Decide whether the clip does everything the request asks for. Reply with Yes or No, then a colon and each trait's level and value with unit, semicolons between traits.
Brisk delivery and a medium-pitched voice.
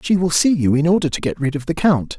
Yes: fast, 330 wpm; medium, 155 Hz